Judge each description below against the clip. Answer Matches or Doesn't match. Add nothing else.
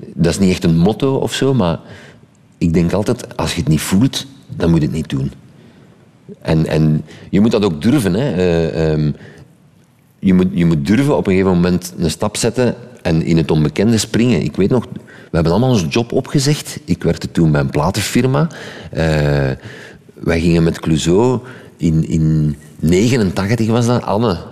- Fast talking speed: Doesn't match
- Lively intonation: Matches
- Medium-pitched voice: Doesn't match